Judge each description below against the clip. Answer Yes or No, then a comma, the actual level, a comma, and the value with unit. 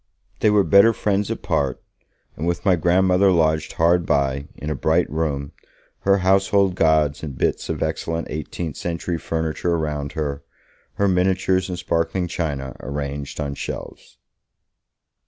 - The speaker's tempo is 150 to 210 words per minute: No, average, 140 wpm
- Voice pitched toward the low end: Yes, very low, 80 Hz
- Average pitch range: Yes, average, 4.0 semitones